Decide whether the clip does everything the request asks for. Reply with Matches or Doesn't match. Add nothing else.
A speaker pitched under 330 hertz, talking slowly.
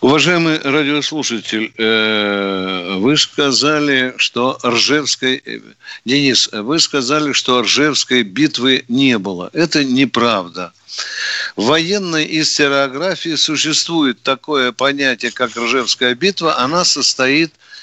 Matches